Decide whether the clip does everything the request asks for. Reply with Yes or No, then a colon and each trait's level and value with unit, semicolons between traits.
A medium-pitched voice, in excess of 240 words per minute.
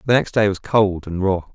No: low, 100 Hz; fast, 270 wpm